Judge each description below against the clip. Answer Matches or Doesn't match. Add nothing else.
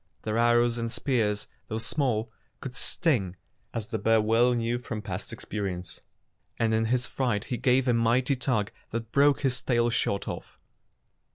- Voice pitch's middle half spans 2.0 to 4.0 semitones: Matches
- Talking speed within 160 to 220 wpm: Matches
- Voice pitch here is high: Doesn't match